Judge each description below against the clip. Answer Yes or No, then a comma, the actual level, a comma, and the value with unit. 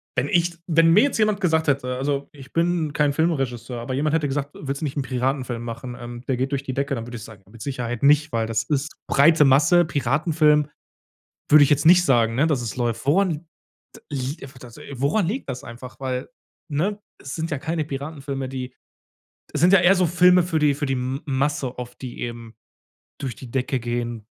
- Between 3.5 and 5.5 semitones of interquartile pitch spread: Yes, average, 3.9 semitones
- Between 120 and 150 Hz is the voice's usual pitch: Yes, medium, 140 Hz